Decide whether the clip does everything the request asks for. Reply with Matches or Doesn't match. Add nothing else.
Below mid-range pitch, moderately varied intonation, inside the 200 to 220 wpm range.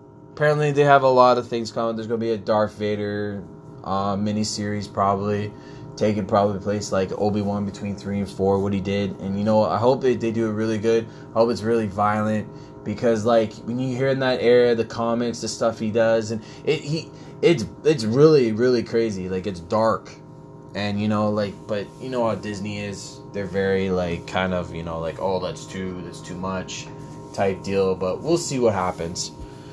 Matches